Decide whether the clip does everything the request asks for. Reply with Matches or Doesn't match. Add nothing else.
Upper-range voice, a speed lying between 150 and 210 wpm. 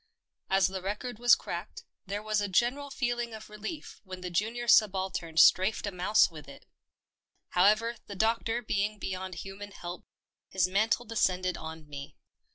Matches